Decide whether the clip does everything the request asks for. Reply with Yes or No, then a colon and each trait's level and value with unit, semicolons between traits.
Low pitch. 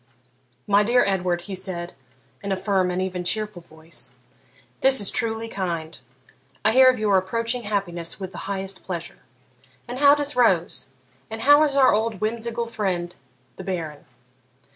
No: high, 195 Hz